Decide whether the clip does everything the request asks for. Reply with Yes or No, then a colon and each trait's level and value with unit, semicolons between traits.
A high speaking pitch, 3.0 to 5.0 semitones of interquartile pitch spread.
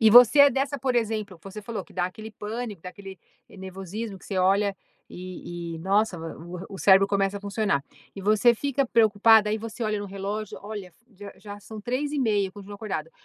No: high, 205 Hz; narrow, 2.5 semitones